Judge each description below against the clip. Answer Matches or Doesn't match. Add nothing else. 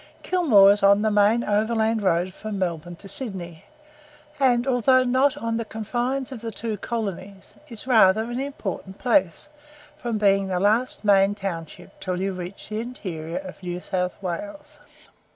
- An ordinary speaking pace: Matches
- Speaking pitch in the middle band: Doesn't match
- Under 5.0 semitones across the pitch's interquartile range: Matches